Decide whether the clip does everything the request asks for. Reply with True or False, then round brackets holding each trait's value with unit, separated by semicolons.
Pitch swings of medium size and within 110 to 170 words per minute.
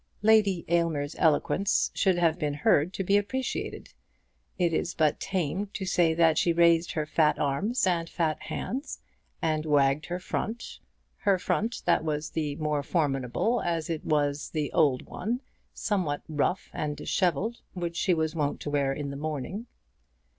True (3.8 semitones; 160 wpm)